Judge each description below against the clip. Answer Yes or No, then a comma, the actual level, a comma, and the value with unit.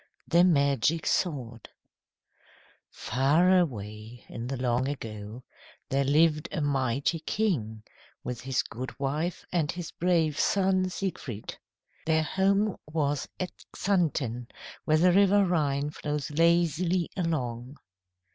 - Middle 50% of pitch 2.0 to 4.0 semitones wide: No, average, 5.2 semitones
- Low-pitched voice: No, medium, 150 Hz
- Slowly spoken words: Yes, slow, 110 wpm